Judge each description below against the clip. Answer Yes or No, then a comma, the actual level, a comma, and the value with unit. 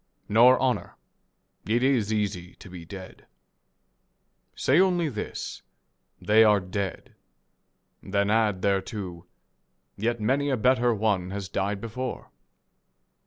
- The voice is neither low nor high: No, low, 105 Hz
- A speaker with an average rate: No, slow, 120 wpm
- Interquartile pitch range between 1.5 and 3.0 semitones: No, average, 3.9 semitones